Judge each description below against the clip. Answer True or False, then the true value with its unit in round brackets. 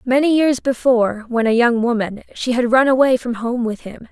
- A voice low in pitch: False (240 Hz)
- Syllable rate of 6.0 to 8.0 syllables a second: False (5.1 syllables/s)